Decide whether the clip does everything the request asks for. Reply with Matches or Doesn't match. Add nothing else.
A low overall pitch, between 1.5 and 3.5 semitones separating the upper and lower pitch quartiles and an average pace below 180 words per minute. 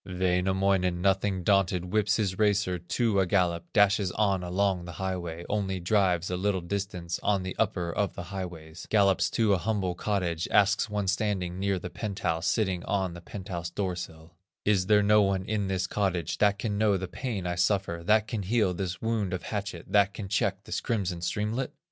Doesn't match